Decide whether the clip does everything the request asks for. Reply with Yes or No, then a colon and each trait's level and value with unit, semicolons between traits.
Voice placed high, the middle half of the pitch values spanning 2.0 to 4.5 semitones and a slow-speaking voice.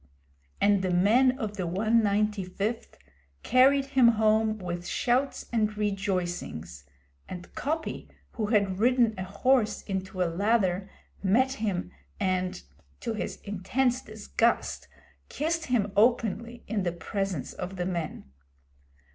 Yes: high, 210 Hz; average, 4.0 semitones; slow, 120 wpm